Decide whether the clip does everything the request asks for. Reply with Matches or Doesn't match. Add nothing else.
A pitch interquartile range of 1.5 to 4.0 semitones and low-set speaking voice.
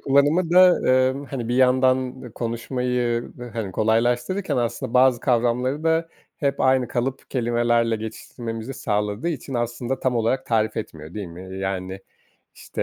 Matches